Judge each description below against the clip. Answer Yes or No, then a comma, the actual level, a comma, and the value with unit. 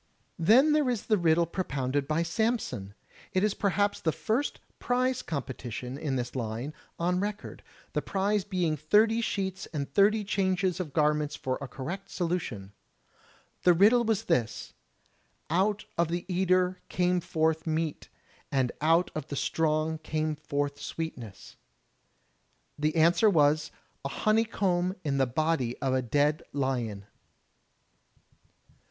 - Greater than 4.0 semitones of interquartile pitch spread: Yes, average, 5.3 semitones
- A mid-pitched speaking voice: Yes, medium, 165 Hz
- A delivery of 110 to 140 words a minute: Yes, slow, 135 wpm